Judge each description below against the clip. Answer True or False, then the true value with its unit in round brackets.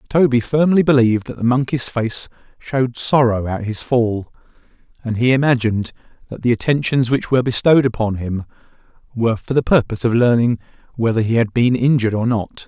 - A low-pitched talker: True (120 Hz)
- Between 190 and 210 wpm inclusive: False (170 wpm)